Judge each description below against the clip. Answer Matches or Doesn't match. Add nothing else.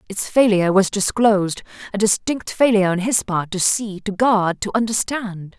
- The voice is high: Matches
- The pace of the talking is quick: Doesn't match